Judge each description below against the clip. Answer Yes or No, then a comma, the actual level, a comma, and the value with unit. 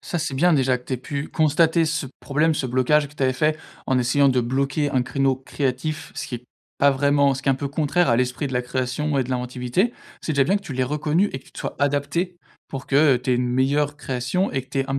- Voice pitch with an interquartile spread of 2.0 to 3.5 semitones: Yes, average, 2.8 semitones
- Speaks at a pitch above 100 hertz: Yes, medium, 140 Hz